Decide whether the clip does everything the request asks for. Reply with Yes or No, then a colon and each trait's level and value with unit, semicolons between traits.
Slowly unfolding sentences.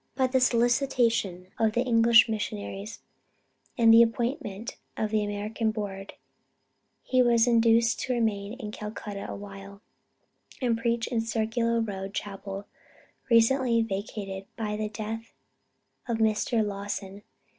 Yes: slow, 125 wpm